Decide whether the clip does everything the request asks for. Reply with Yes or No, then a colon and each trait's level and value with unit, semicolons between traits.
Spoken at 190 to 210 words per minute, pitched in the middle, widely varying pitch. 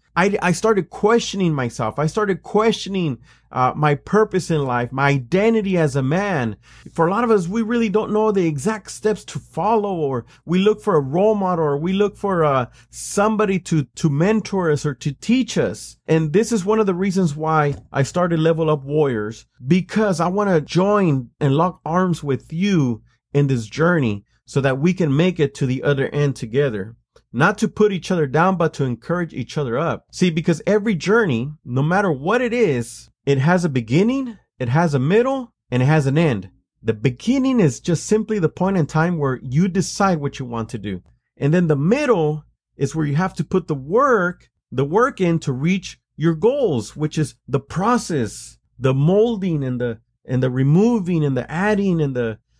Yes: average, 200 wpm; medium, 160 Hz; wide, 6.1 semitones